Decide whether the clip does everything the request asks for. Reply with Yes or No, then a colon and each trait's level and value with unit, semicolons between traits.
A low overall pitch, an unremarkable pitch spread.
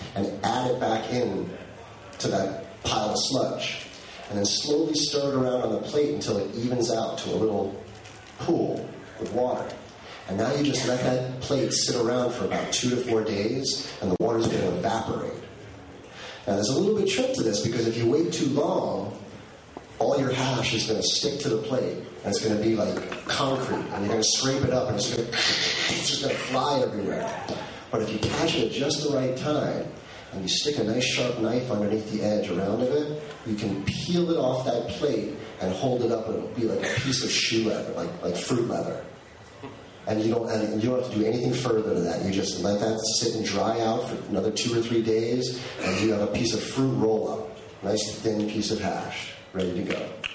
Yes: low, 115 Hz; average, 3.1 semitones